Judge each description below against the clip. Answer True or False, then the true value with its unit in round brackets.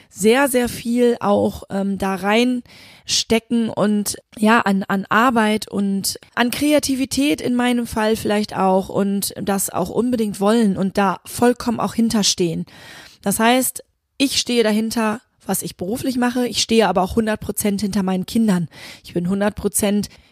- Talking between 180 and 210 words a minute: False (155 wpm)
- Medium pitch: False (215 Hz)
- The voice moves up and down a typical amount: True (3.2 semitones)